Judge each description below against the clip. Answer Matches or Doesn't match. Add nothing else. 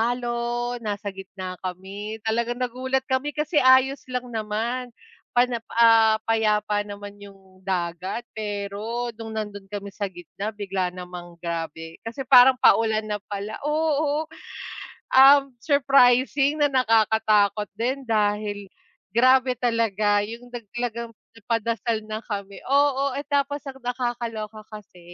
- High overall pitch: Matches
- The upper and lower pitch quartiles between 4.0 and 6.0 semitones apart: Doesn't match